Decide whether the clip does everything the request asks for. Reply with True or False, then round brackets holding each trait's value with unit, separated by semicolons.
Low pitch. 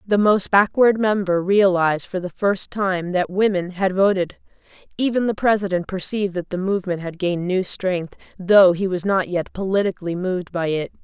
False (190 Hz)